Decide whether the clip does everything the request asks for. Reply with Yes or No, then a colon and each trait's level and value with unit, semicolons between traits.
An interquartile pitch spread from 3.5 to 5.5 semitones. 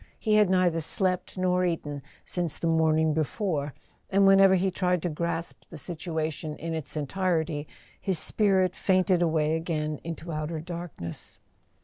No: average, 2.8 semitones